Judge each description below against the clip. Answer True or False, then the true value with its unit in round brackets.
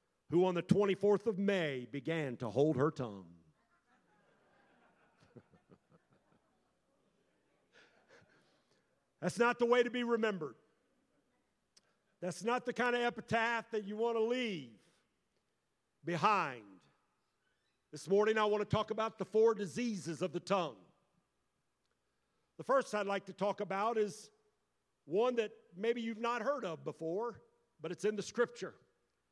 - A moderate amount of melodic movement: False (5.8 semitones)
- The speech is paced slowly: True (130 wpm)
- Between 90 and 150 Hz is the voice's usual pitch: False (205 Hz)